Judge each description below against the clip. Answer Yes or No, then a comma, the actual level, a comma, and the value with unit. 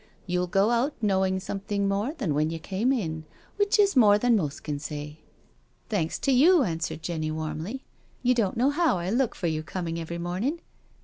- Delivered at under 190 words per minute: No, average, 200 wpm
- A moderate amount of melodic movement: No, wide, 7.0 semitones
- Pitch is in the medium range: No, high, 195 Hz